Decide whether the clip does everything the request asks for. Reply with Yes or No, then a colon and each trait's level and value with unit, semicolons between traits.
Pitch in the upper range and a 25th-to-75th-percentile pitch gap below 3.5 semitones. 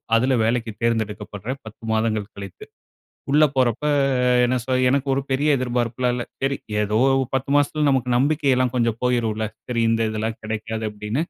No: low, 120 Hz; average, 3.1 semitones